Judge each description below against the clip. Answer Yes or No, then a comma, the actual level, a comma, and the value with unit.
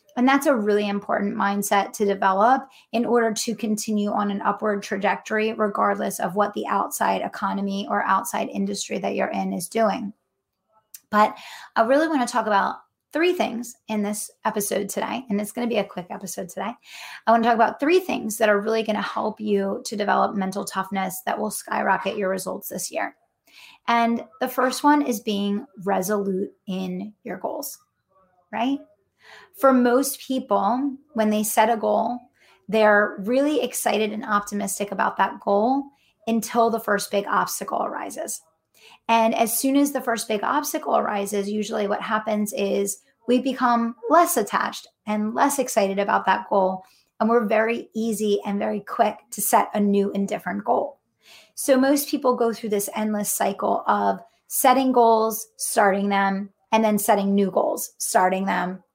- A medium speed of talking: Yes, average, 170 wpm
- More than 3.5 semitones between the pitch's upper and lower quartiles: No, average, 2.8 semitones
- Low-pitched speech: No, high, 215 Hz